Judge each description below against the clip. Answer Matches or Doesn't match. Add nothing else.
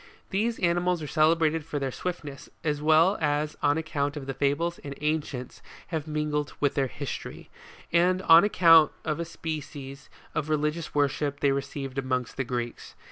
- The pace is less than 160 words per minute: Doesn't match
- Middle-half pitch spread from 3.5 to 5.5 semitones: Doesn't match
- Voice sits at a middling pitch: Matches